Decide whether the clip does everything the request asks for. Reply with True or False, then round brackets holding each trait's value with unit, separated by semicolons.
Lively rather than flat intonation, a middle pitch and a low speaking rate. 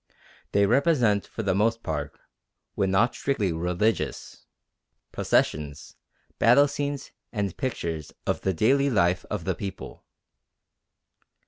False (5.9 semitones; 105 Hz; 115 wpm)